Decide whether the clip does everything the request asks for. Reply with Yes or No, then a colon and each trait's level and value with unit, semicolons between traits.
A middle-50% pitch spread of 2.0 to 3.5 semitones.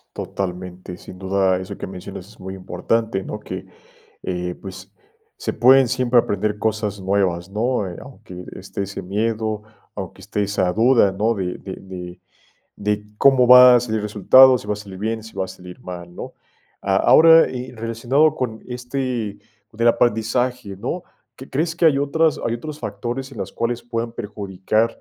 No: average, 4.3 semitones